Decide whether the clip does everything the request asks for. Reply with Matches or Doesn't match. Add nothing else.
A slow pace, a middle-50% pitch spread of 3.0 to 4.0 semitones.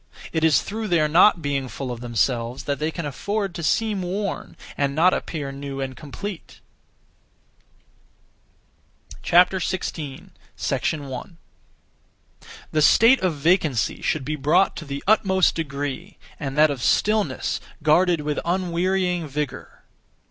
Doesn't match